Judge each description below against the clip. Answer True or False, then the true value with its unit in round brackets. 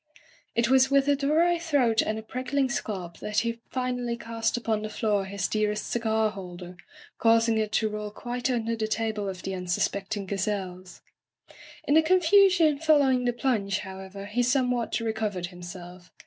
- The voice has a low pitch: False (220 Hz)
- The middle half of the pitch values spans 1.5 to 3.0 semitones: False (4.1 semitones)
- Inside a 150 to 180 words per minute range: True (165 wpm)